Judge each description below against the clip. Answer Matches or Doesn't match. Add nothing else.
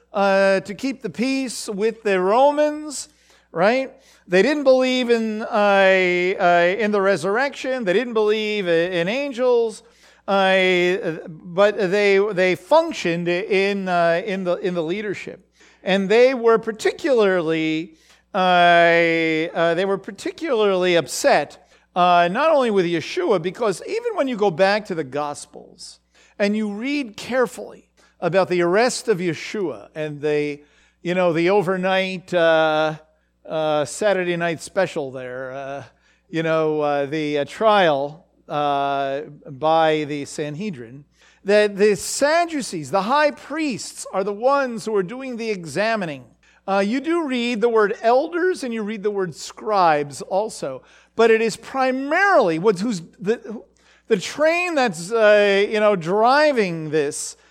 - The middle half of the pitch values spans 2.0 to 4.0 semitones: Doesn't match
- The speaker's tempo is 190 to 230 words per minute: Doesn't match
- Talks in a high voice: Matches